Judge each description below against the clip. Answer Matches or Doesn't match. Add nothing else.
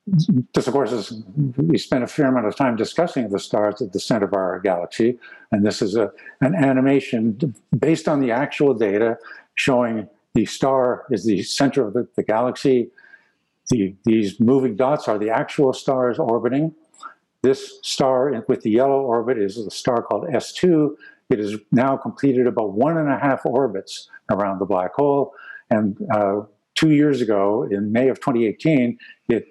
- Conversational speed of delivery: Matches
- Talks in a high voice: Doesn't match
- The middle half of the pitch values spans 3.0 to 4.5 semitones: Matches